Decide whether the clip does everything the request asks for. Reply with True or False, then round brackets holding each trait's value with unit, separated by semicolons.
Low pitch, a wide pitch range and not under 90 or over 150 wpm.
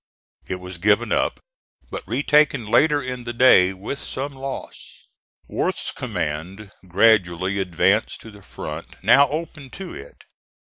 True (110 Hz; 6.6 semitones; 135 wpm)